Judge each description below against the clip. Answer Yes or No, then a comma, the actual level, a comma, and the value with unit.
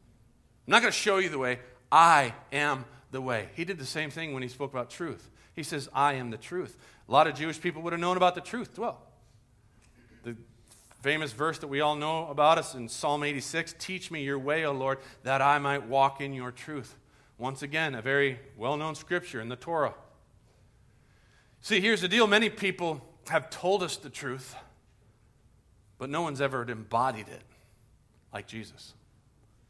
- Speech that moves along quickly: No, average, 190 wpm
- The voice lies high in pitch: No, low, 135 Hz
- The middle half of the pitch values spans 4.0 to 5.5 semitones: Yes, average, 4.9 semitones